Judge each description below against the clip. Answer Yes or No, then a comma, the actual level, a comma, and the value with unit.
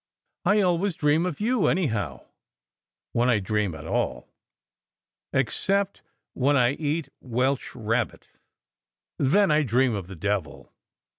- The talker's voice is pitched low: Yes, low, 130 Hz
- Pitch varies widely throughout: Yes, wide, 7.8 semitones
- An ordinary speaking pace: No, slow, 130 wpm